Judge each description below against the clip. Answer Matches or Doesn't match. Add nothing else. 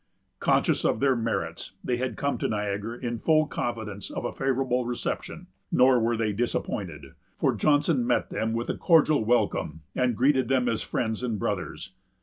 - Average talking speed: Matches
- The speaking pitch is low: Matches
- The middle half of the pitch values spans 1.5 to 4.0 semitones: Matches